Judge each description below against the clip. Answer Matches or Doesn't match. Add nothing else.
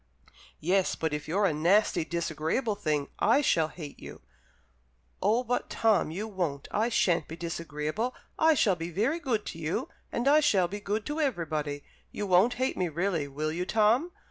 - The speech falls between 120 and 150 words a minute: Doesn't match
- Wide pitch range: Matches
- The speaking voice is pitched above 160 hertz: Matches